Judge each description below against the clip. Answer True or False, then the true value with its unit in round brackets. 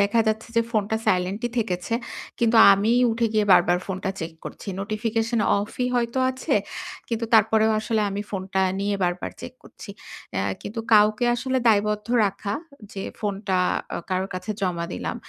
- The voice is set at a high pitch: True (210 Hz)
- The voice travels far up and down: False (2.7 semitones)